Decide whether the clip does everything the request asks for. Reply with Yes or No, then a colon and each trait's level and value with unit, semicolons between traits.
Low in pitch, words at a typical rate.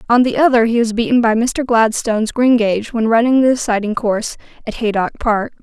No: high, 230 Hz; average, 190 wpm